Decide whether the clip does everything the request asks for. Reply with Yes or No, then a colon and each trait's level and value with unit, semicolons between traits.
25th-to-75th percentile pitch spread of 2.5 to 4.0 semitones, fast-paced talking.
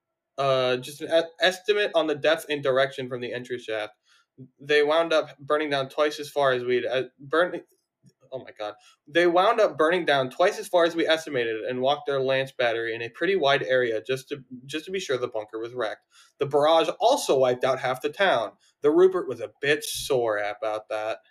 No: average, 4.7 semitones; fast, 210 wpm